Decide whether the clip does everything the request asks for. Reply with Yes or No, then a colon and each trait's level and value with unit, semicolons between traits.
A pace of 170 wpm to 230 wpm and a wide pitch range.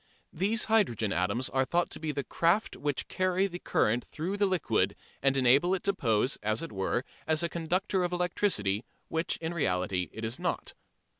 Yes: average, 190 wpm; wide, 7.5 semitones